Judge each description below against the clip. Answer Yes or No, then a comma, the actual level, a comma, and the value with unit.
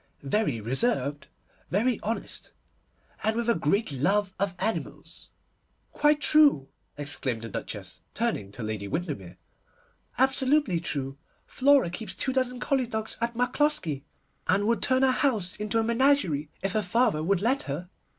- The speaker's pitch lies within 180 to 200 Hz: No, high, 210 Hz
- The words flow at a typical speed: Yes, average, 150 wpm